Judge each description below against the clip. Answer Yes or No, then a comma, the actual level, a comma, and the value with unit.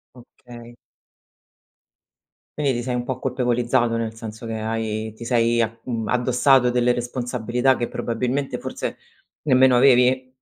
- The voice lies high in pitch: No, low, 120 Hz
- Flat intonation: Yes, narrow, 1.6 semitones